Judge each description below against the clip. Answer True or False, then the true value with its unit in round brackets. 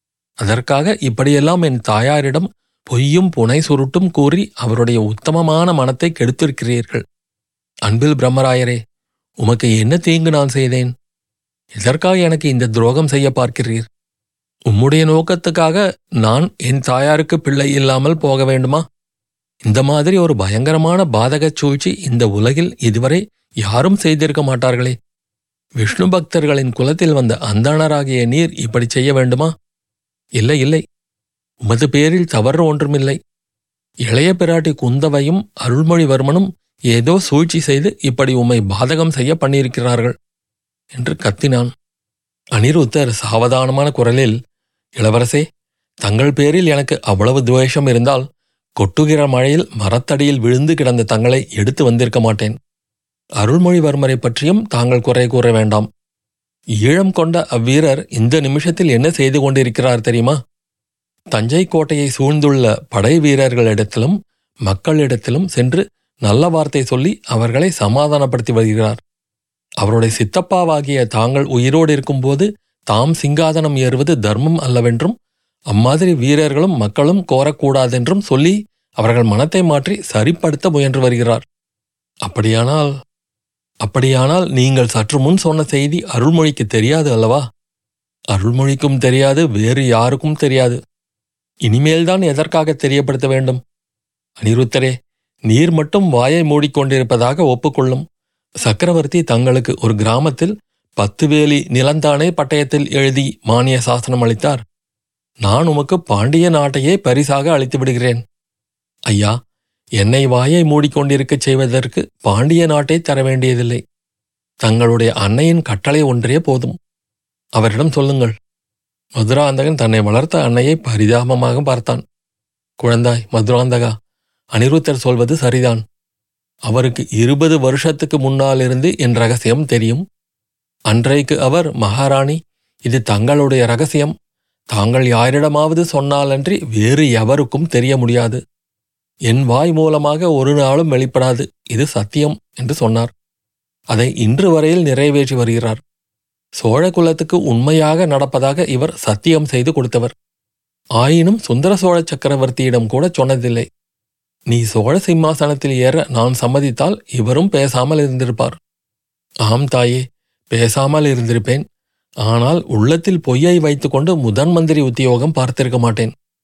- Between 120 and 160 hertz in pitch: True (135 Hz)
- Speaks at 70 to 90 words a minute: False (105 wpm)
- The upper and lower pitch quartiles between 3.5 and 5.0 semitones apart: True (4.5 semitones)